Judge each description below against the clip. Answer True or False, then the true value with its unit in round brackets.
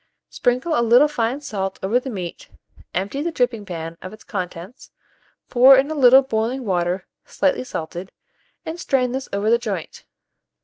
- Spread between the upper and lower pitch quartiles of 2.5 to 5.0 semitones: False (5.6 semitones)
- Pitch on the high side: True (235 Hz)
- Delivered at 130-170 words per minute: True (165 wpm)